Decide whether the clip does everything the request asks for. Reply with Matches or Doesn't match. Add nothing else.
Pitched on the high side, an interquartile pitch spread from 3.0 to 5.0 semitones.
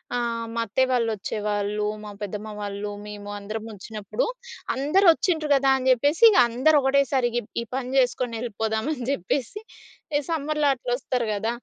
Matches